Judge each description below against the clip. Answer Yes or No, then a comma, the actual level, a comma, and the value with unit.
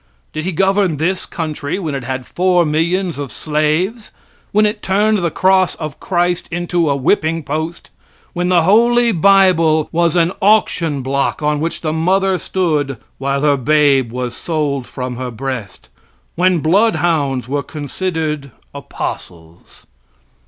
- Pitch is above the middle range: No, medium, 160 Hz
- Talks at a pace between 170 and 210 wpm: No, average, 145 wpm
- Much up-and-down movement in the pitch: No, average, 4.5 semitones